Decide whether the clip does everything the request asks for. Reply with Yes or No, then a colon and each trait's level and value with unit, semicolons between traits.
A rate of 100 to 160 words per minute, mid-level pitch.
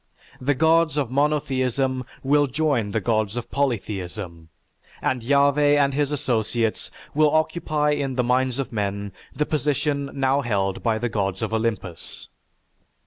No: average, 140 wpm; low, 130 Hz